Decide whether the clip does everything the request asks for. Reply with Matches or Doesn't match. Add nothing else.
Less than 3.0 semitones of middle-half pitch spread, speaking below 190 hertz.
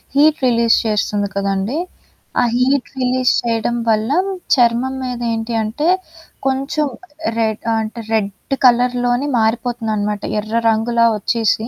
Doesn't match